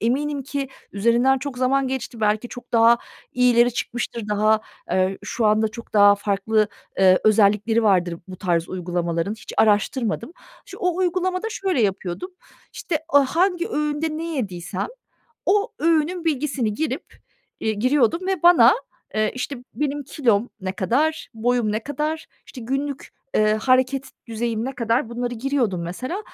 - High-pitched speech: Yes, high, 240 Hz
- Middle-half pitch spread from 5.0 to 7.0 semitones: Yes, wide, 5.5 semitones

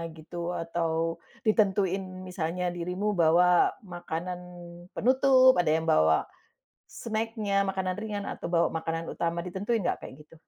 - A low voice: No, medium, 180 Hz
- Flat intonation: No, average, 3.6 semitones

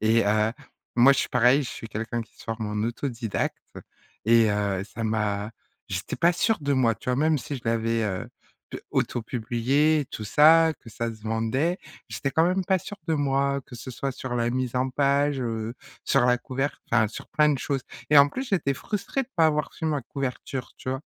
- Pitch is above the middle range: No, low, 125 Hz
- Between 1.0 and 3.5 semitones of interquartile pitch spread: No, average, 4.3 semitones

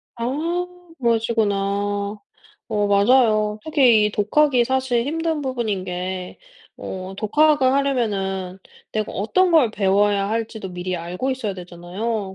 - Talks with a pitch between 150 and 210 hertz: No, high, 220 Hz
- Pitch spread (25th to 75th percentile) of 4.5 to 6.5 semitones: Yes, average, 5.2 semitones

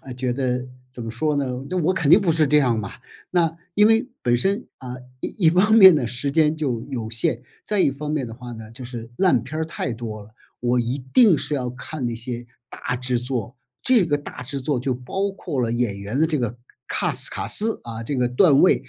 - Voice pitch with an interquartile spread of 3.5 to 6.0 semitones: Yes, average, 4.8 semitones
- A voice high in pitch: No, low, 130 Hz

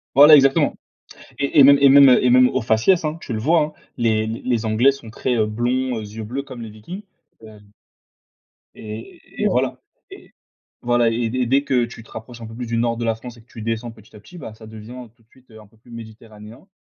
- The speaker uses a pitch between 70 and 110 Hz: No, low, 120 Hz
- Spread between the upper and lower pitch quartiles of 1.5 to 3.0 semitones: Yes, average, 2.7 semitones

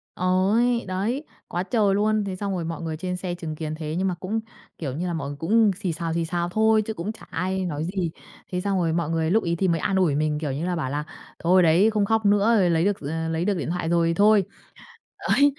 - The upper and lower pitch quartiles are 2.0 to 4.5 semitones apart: Yes, average, 3.8 semitones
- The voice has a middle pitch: Yes, medium, 180 Hz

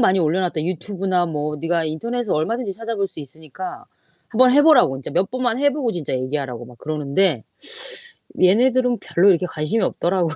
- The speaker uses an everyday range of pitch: No, wide, 7.0 semitones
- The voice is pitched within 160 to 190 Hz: Yes, medium, 185 Hz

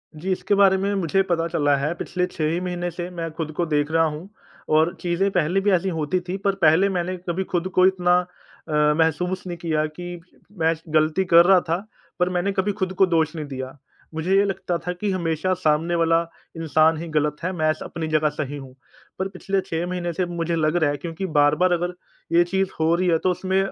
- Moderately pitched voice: Yes, medium, 170 Hz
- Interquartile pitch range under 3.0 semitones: Yes, narrow, 2.6 semitones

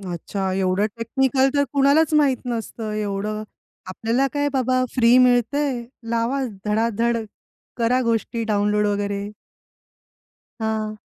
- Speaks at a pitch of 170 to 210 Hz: No, high, 230 Hz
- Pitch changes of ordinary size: Yes, average, 3.6 semitones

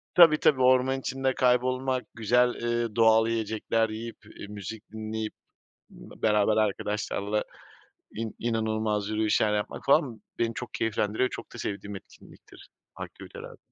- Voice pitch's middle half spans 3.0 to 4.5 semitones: No, narrow, 2.5 semitones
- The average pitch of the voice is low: Yes, low, 110 Hz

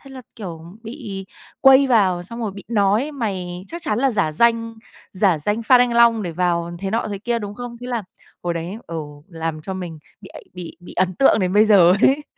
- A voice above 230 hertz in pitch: No, high, 205 Hz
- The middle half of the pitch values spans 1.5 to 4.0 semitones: No, average, 4.7 semitones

